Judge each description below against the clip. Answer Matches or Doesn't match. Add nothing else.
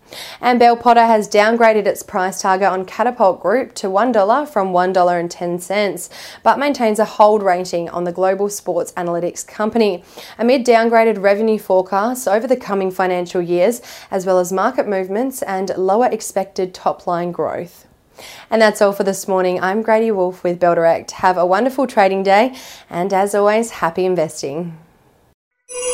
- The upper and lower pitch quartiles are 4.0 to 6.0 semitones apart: Doesn't match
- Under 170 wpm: Matches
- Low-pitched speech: Doesn't match